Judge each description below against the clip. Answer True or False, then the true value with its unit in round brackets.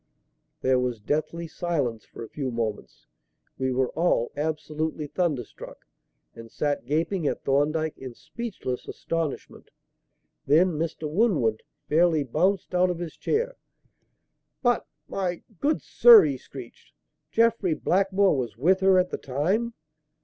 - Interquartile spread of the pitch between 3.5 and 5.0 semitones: False (5.6 semitones)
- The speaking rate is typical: False (130 wpm)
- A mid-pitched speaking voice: True (160 Hz)